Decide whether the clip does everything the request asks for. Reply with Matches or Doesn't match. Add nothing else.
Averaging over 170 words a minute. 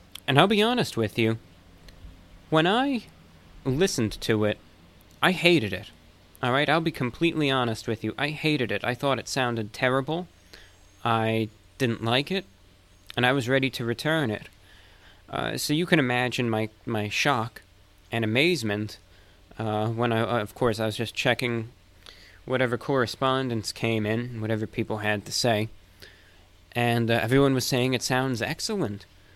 Doesn't match